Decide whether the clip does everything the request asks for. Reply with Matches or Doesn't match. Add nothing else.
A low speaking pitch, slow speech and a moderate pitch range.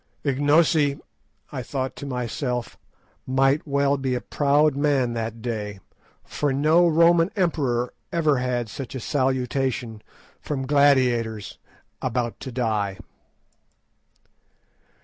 Matches